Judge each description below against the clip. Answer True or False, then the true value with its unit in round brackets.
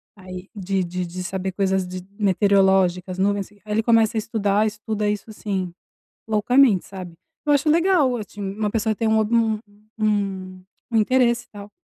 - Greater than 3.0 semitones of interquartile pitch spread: False (2.6 semitones)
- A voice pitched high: True (205 Hz)